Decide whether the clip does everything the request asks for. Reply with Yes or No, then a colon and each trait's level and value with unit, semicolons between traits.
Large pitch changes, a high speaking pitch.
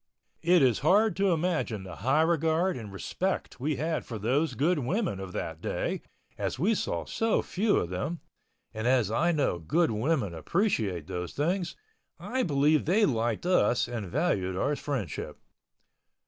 No: wide, 8.0 semitones; medium, 145 Hz